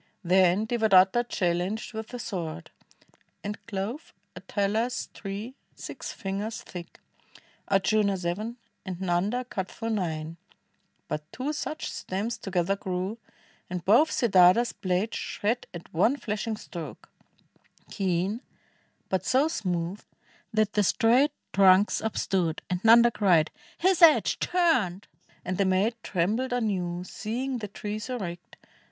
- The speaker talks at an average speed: No, slow, 125 wpm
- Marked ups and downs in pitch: No, average, 4.1 semitones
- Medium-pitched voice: No, high, 200 Hz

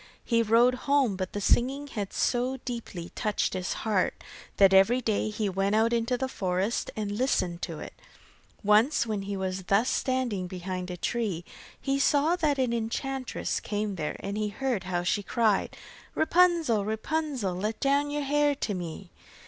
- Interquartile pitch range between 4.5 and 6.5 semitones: Yes, average, 5.2 semitones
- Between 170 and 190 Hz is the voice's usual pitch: No, high, 220 Hz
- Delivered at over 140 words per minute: Yes, average, 170 wpm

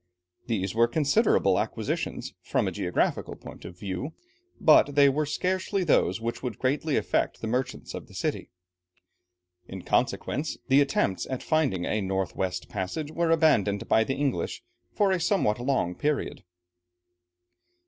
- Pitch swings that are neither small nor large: No, wide, 7.3 semitones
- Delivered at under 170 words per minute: Yes, average, 150 wpm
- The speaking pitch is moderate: No, low, 130 Hz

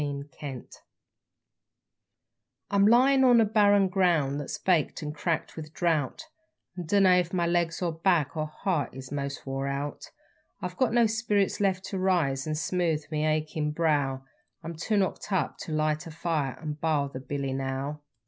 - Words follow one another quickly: No, average, 170 wpm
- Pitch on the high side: No, medium, 160 Hz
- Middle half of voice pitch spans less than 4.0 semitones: No, average, 4.4 semitones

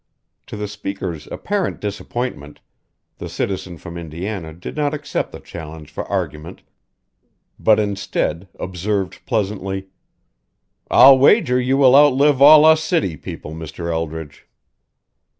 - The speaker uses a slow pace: Yes, slow, 120 wpm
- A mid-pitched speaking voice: No, low, 100 Hz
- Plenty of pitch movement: Yes, wide, 8.0 semitones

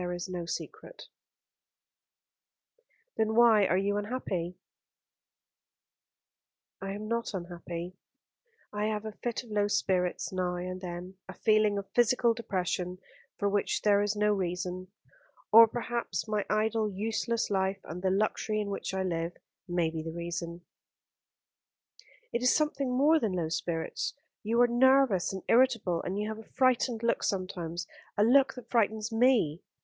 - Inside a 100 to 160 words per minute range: Yes, average, 150 wpm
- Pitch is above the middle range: Yes, high, 205 Hz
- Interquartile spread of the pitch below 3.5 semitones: No, average, 4.0 semitones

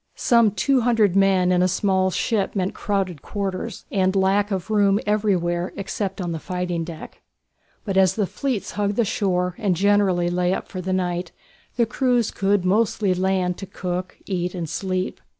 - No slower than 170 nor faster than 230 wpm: Yes, average, 175 wpm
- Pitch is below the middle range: No, high, 190 Hz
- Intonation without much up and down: Yes, narrow, 2.2 semitones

